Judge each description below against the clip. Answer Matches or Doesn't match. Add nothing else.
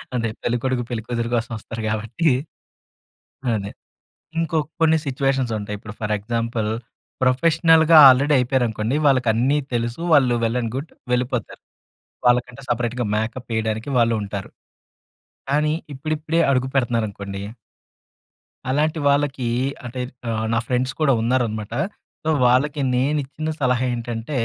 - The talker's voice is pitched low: Matches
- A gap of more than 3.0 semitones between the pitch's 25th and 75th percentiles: Matches